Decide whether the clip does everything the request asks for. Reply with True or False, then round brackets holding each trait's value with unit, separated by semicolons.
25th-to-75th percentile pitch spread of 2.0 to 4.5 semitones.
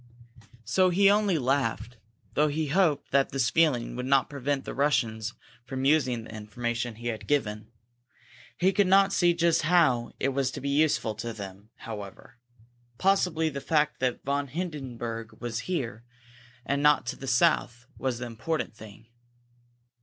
False (4.9 semitones)